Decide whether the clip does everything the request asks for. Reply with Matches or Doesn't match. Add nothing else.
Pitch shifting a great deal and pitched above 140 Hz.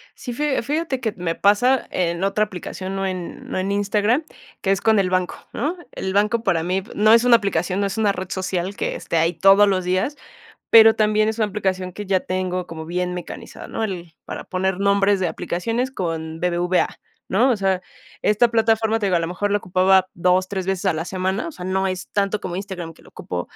Doesn't match